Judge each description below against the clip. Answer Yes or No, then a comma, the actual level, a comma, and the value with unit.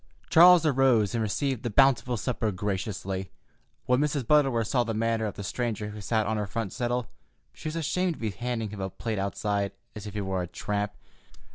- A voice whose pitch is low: Yes, low, 110 Hz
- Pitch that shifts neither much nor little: Yes, average, 3.6 semitones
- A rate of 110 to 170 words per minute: No, fast, 205 wpm